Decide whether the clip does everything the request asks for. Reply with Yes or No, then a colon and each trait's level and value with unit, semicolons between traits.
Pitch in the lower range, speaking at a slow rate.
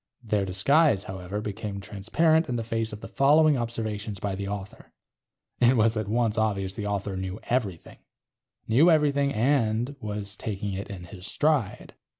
No: low, 110 Hz; average, 160 wpm